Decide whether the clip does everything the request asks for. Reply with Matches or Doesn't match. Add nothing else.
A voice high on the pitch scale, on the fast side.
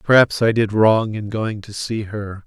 Doesn't match